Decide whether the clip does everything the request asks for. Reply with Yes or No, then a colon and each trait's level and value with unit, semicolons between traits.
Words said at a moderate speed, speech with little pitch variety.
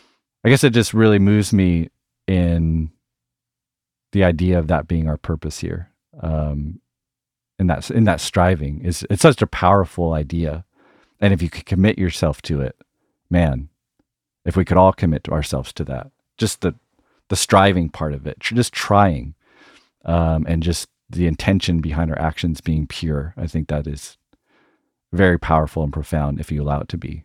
No: average, 170 wpm; average, 3.4 semitones